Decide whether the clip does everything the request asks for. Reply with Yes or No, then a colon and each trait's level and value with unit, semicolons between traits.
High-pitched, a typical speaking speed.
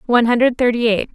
No: high, 235 Hz; fast, 210 wpm